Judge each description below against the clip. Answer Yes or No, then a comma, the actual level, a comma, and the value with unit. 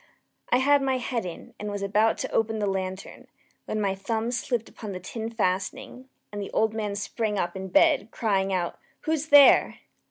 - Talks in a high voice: Yes, high, 215 Hz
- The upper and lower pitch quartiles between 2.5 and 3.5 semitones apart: No, average, 4.0 semitones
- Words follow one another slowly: No, average, 190 wpm